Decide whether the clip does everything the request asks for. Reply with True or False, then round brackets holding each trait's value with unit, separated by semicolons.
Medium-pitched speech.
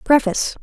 False (245 Hz)